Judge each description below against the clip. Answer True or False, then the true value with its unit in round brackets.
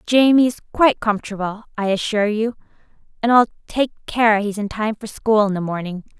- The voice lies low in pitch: False (215 Hz)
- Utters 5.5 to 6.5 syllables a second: True (5.8 syllables/s)